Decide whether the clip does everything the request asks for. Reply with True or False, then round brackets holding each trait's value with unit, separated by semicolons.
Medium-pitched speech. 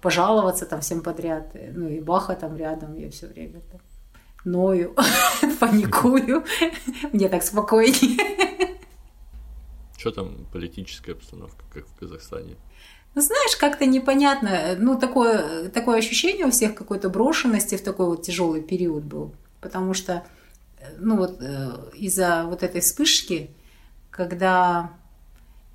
True (180 Hz)